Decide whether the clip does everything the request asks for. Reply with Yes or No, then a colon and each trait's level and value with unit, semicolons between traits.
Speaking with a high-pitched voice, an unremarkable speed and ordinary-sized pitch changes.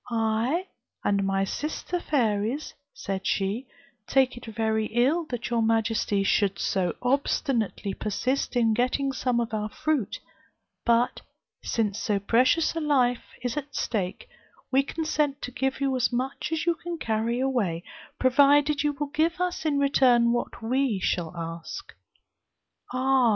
Yes: high, 245 Hz; average, 145 wpm; average, 4.3 semitones